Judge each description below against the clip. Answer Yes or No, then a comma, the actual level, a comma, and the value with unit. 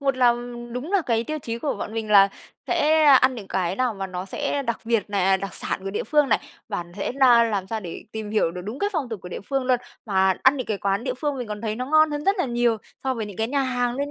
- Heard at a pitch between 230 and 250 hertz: Yes, high, 235 Hz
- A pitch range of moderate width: Yes, average, 4.8 semitones